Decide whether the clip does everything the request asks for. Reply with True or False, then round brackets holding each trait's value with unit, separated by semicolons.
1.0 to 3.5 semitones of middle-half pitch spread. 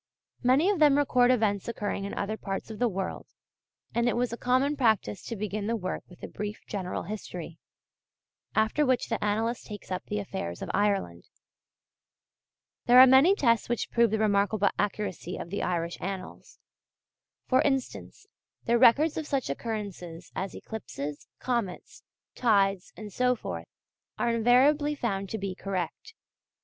False (4.1 semitones)